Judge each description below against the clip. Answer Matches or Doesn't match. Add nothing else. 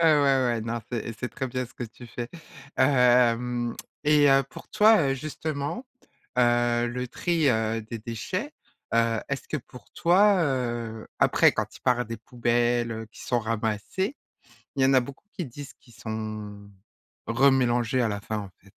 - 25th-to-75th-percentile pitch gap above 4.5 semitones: Doesn't match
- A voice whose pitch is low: Matches